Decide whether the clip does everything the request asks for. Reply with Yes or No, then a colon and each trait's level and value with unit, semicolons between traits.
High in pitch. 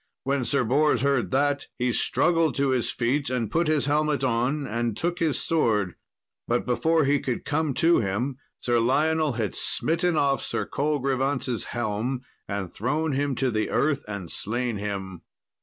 No: low, 135 Hz